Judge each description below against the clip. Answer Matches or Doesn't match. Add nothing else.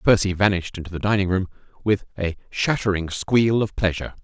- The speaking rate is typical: Matches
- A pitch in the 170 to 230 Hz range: Doesn't match